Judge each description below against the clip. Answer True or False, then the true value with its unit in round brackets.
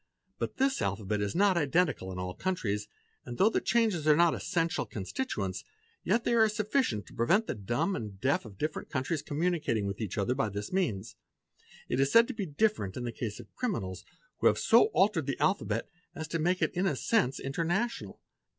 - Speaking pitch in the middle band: True (155 Hz)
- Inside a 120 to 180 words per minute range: False (205 wpm)